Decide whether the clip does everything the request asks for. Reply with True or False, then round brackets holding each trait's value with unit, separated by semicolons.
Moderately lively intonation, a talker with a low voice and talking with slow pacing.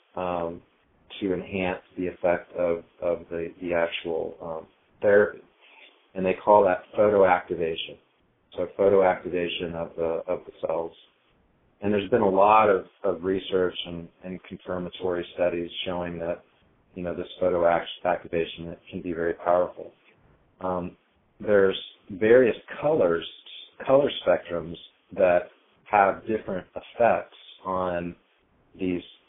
False (1.7 semitones; 90 Hz; 120 wpm)